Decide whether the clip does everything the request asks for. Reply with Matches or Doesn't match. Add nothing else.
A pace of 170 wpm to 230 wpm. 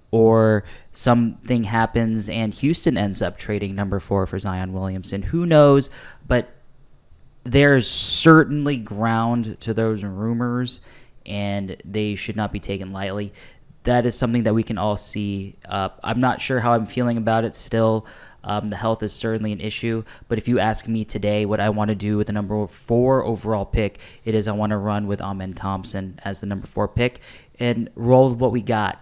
Matches